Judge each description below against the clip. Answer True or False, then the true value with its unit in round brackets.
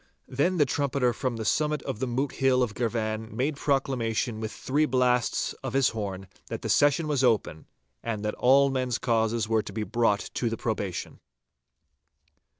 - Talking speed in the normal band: True (175 wpm)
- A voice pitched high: False (125 Hz)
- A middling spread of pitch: True (3.4 semitones)